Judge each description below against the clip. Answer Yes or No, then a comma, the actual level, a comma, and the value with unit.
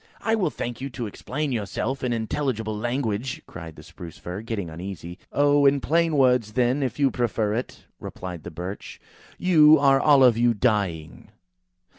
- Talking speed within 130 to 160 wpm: No, average, 170 wpm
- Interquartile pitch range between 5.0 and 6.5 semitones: Yes, average, 5.3 semitones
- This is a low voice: Yes, low, 120 Hz